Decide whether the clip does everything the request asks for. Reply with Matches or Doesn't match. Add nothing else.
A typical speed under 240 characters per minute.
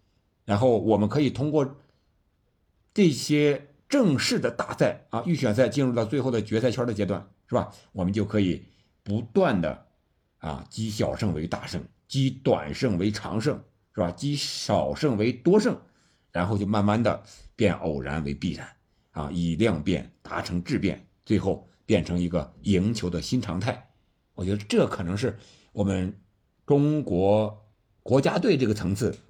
Matches